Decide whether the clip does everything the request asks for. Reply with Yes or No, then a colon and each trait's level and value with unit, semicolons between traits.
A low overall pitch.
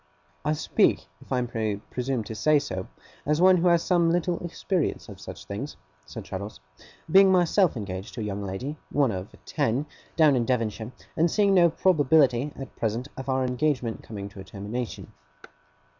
Yes: low, 130 Hz